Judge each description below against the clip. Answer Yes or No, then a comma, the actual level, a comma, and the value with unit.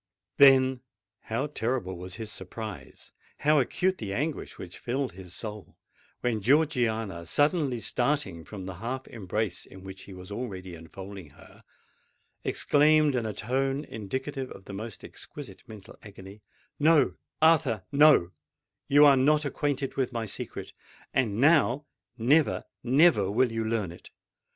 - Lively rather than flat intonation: Yes, wide, 6.0 semitones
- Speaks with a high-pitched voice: No, low, 120 Hz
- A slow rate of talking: Yes, slow, 130 wpm